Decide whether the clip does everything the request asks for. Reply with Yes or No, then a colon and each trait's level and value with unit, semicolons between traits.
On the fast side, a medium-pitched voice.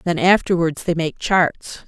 No: average, 160 wpm; medium, 170 Hz